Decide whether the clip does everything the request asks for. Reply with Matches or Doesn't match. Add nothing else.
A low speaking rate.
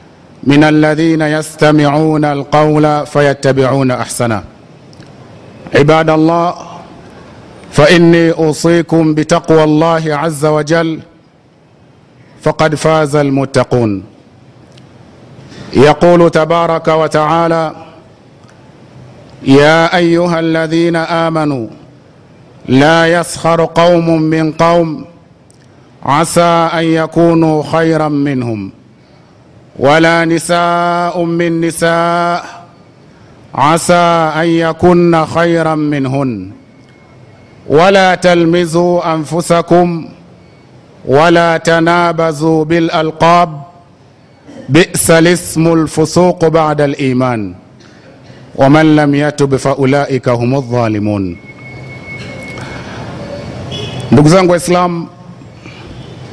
Matches